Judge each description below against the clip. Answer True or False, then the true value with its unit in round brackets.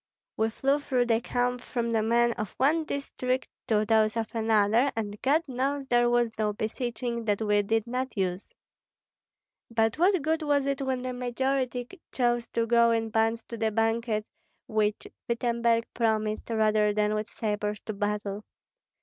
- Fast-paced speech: False (165 wpm)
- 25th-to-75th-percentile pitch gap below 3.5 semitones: True (2.6 semitones)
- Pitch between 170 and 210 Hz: False (230 Hz)